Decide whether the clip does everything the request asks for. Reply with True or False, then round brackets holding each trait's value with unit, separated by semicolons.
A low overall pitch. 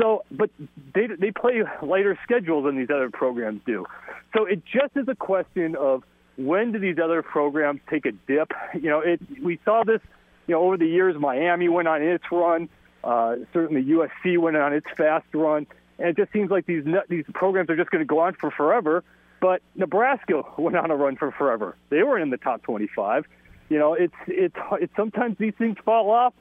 False (175 Hz)